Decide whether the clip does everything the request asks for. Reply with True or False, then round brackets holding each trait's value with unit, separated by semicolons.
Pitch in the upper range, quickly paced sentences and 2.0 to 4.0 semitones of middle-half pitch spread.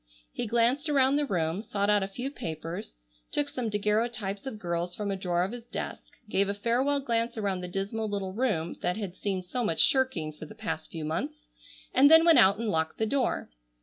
False (210 Hz; 215 wpm; 5.3 semitones)